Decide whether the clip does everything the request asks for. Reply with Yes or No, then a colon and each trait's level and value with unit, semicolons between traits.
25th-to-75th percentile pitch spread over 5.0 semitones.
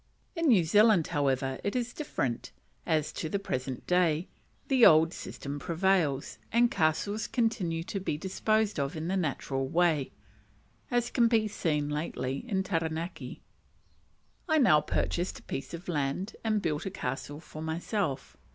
Yes: wide, 5.6 semitones